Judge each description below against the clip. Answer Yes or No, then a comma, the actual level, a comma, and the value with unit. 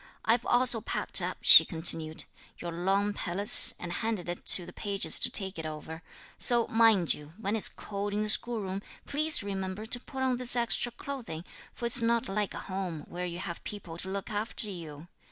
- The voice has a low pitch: No, high, 200 Hz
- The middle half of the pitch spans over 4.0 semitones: Yes, average, 4.5 semitones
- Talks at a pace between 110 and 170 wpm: No, average, 190 wpm